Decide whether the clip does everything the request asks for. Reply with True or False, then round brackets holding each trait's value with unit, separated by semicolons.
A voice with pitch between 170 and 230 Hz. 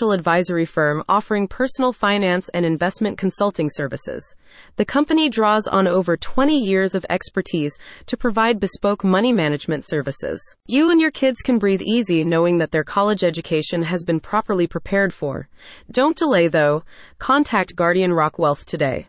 True (190 Hz)